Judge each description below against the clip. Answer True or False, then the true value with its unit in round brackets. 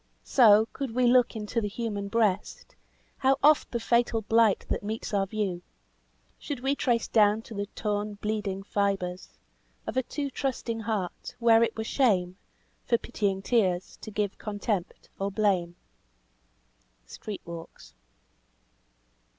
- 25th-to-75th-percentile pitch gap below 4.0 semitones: True (2.8 semitones)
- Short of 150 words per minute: True (140 wpm)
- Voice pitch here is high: True (215 Hz)